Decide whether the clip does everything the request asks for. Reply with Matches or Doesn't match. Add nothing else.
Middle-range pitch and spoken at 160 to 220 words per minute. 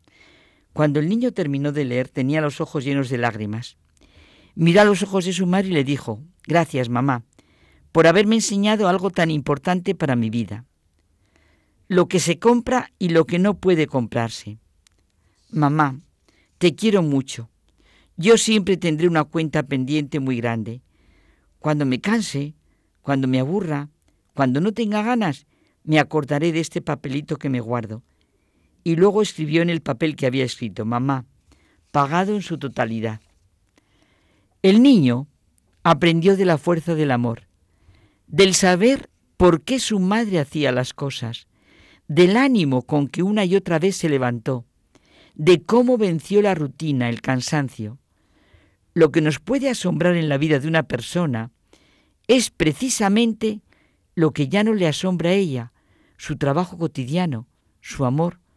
Doesn't match